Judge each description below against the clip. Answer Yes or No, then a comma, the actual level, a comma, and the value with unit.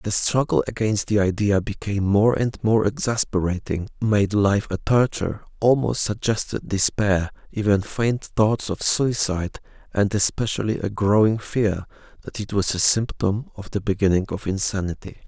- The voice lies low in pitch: Yes, low, 105 Hz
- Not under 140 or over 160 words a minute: Yes, average, 145 wpm